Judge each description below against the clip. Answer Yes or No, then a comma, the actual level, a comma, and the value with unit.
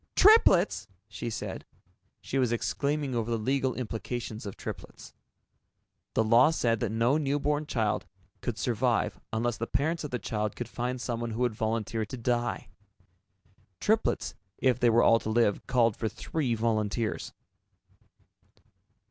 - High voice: No, low, 120 Hz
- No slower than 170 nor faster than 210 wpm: No, average, 145 wpm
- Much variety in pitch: No, average, 2.8 semitones